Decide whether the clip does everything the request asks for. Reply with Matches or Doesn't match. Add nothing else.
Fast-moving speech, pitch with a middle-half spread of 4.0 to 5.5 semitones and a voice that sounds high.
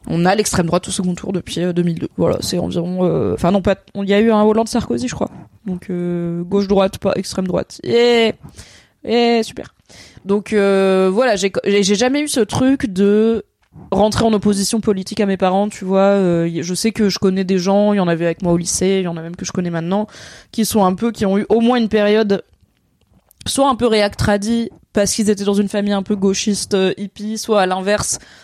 Doesn't match